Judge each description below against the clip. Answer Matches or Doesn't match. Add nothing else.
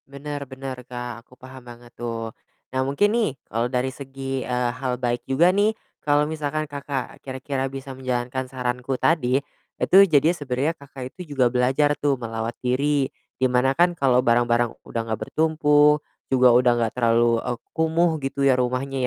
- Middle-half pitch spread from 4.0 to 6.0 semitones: Doesn't match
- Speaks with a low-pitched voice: Matches